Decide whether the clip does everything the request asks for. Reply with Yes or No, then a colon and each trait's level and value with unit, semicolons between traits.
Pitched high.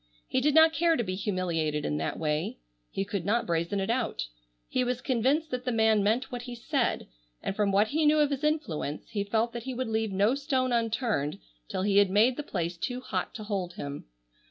Yes: high, 220 Hz